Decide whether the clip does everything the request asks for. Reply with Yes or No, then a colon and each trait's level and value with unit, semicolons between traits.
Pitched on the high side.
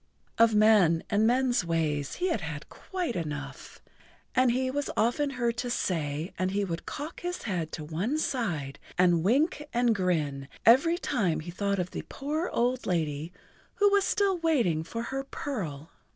Yes: high, 210 Hz